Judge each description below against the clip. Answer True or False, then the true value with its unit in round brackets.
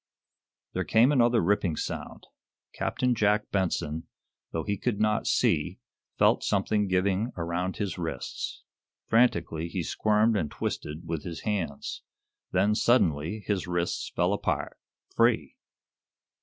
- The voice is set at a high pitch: False (95 Hz)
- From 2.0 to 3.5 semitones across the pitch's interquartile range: False (4.1 semitones)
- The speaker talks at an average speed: False (125 wpm)